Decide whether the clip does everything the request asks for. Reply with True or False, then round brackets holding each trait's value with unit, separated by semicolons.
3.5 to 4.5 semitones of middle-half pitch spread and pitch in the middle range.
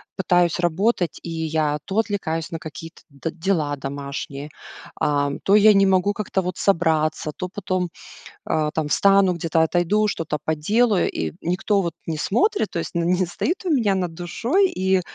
True (3.9 semitones; 175 Hz)